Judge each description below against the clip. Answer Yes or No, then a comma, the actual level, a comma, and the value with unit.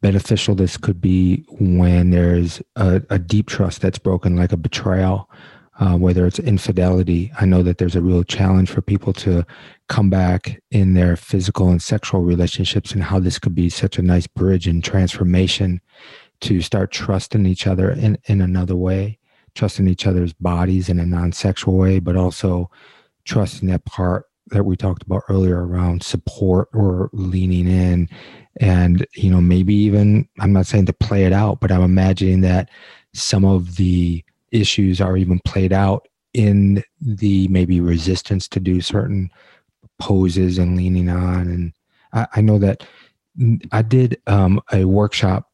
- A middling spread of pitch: No, narrow, 2.0 semitones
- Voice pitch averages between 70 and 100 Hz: Yes, very low, 95 Hz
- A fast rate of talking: No, average, 165 wpm